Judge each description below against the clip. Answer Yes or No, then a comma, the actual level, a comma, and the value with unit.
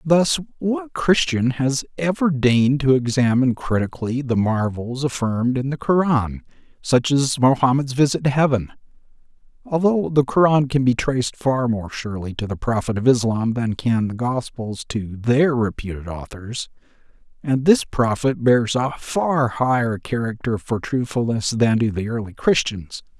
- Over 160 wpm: No, average, 150 wpm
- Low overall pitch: Yes, low, 125 Hz